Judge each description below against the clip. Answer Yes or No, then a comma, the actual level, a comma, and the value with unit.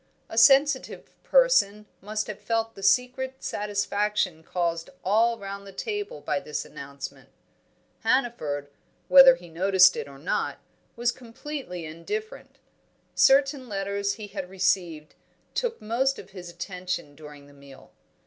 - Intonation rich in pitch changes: Yes, wide, 6.2 semitones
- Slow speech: Yes, slow, 130 wpm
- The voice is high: Yes, high, 200 Hz